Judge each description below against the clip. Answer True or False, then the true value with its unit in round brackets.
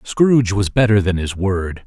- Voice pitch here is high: False (100 Hz)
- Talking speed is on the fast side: False (195 wpm)